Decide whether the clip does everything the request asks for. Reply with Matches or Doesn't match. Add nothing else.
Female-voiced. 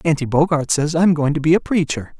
Doesn't match